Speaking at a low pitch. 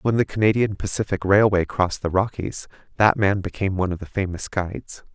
Yes: low, 100 Hz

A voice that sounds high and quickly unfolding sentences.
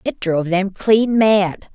No: high, 200 Hz; average, 170 wpm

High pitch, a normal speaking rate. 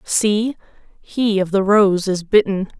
Yes: high, 200 Hz; average, 150 wpm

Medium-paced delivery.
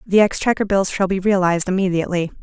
Yes: average, 175 wpm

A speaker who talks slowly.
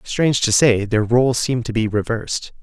No: fast, 205 wpm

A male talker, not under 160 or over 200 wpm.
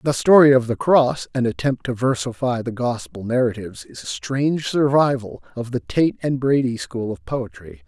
Yes: male; average, 185 wpm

